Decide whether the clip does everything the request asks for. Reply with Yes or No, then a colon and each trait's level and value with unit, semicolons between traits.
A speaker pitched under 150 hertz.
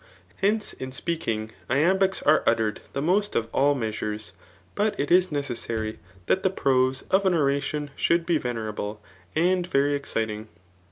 Yes: medium, 140 Hz